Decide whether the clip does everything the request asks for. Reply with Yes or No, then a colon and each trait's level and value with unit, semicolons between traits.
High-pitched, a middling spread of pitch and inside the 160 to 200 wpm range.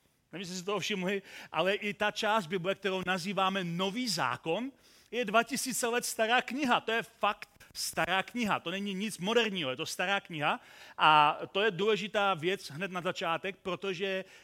Yes: high, 195 Hz; average, 3.2 semitones; fast, 170 wpm